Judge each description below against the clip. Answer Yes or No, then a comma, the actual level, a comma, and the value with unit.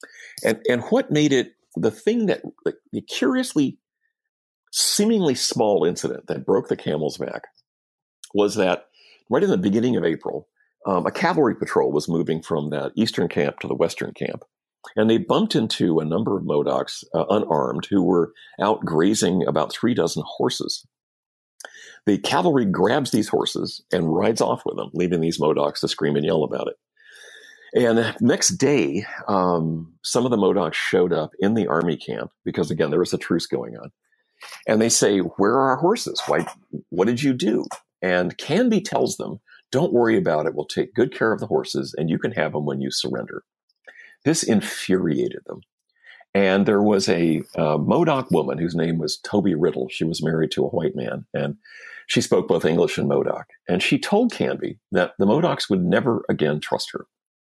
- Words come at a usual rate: Yes, average, 185 wpm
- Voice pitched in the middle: No, low, 115 Hz